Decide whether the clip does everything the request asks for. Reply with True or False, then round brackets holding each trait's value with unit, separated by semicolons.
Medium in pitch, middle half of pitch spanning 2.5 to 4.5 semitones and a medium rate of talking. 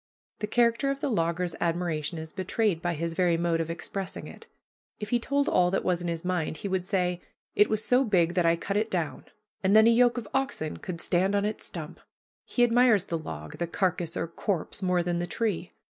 False (180 Hz; 4.2 semitones; 220 wpm)